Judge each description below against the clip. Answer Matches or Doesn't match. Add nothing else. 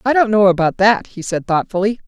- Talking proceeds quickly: Matches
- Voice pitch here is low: Doesn't match